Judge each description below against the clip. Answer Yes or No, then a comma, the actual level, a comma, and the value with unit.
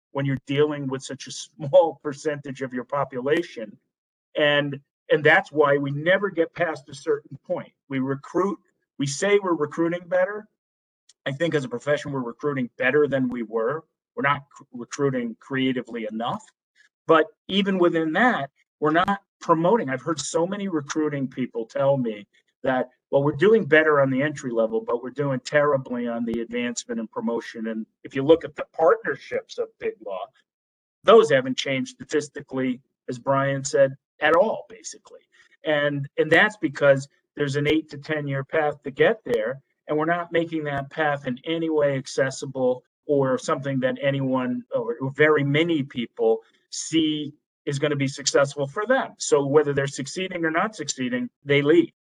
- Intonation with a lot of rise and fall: No, average, 3.7 semitones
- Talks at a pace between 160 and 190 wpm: Yes, average, 170 wpm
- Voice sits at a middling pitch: Yes, medium, 145 Hz